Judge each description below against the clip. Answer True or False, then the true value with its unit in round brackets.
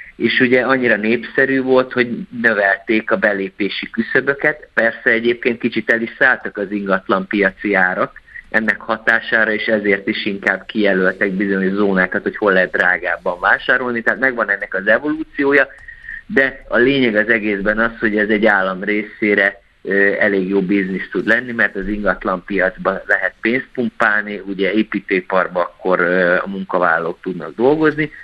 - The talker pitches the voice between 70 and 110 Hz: True (105 Hz)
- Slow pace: False (145 wpm)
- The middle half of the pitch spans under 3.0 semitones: False (3.5 semitones)